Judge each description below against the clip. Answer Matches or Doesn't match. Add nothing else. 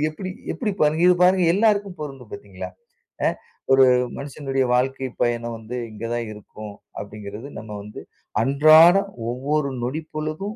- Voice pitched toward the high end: Doesn't match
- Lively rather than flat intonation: Matches